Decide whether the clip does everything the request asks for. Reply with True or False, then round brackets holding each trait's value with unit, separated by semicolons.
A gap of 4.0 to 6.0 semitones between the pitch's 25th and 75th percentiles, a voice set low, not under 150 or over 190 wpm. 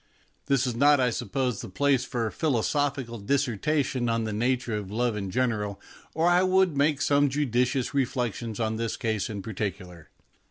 True (4.4 semitones; 125 Hz; 185 wpm)